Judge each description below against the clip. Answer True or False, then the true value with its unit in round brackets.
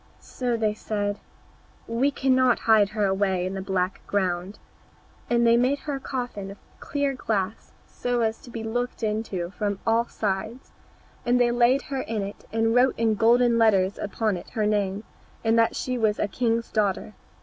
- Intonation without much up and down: False (3.0 semitones)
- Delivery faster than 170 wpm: True (180 wpm)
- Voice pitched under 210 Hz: False (225 Hz)